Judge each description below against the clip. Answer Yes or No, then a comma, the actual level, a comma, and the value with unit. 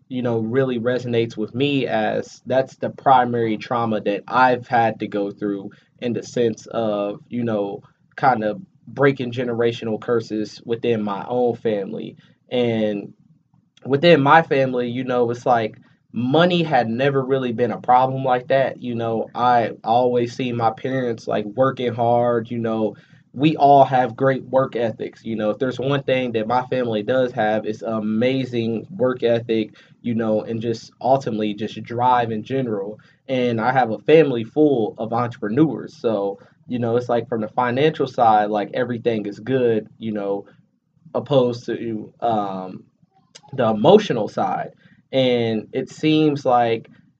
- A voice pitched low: Yes, low, 120 Hz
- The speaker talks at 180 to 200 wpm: No, average, 160 wpm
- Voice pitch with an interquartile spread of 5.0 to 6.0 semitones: No, average, 2.9 semitones